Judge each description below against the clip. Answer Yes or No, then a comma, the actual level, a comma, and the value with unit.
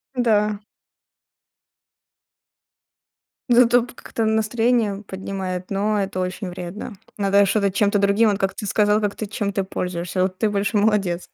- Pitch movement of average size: No, narrow, 2.0 semitones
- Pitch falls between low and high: No, high, 200 Hz